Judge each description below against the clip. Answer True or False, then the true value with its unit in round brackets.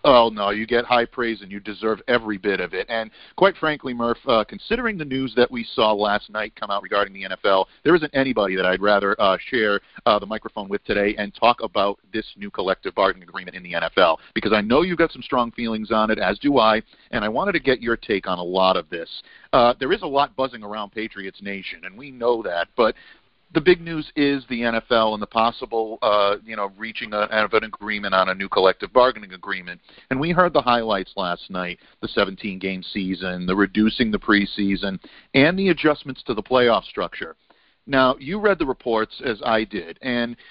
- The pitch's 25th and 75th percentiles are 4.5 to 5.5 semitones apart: False (4.1 semitones)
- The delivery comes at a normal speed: False (215 wpm)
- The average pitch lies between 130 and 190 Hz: False (110 Hz)